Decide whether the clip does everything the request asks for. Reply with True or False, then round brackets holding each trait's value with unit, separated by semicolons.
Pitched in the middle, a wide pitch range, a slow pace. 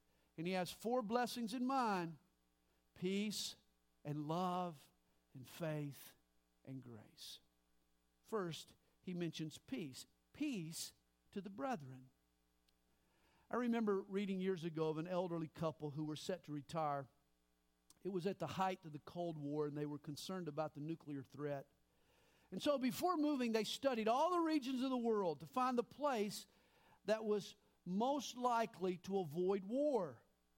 False (170 Hz; 7.9 semitones; 150 wpm)